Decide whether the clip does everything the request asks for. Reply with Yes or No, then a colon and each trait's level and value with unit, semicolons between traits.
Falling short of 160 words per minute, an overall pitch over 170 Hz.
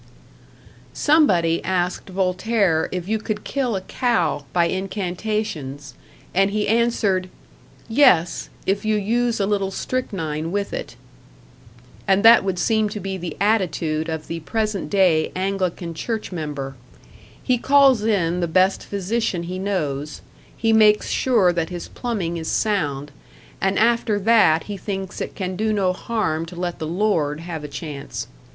Yes: average, 150 wpm; high, 190 Hz